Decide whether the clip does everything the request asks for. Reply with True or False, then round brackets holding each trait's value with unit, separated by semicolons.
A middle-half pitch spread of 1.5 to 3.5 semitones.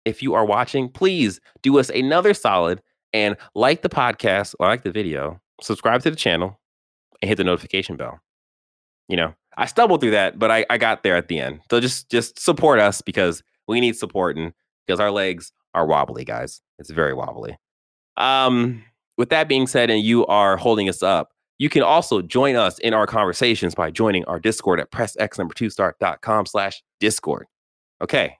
False (4.3 semitones)